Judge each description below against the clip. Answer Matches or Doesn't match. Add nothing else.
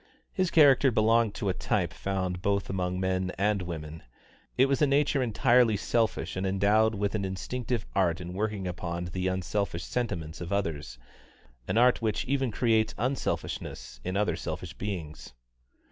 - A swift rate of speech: Doesn't match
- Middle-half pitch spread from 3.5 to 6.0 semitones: Matches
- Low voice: Matches